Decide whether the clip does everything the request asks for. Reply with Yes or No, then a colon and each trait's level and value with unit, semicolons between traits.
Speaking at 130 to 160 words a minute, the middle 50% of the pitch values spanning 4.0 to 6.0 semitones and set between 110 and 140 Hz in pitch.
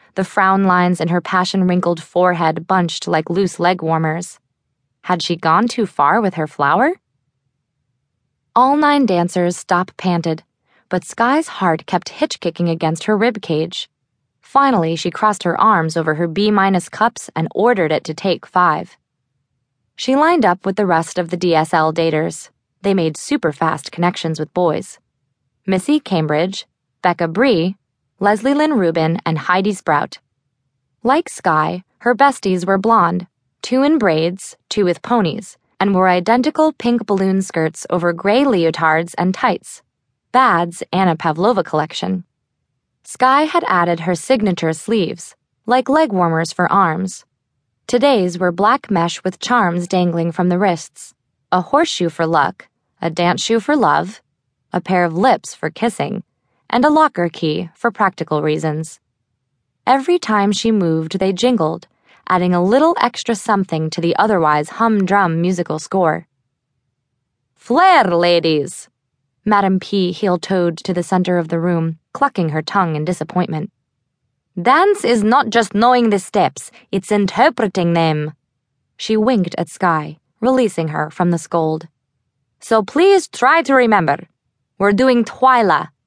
No: average, 140 wpm; average, 5.0 semitones; medium, 180 Hz